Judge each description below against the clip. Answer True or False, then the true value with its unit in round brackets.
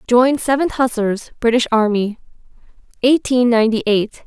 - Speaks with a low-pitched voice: False (235 Hz)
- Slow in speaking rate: True (115 wpm)